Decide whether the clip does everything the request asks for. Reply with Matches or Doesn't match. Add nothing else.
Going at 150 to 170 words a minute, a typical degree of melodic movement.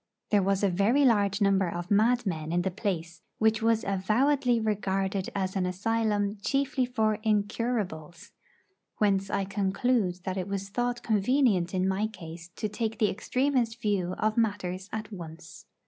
Matches